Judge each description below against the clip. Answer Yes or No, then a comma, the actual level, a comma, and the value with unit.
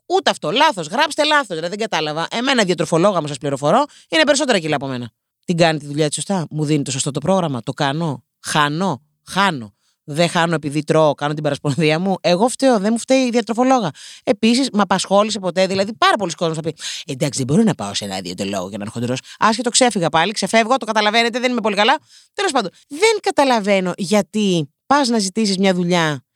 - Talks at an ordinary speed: No, fast, 205 wpm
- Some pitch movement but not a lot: No, wide, 7.3 semitones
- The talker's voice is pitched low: No, medium, 185 Hz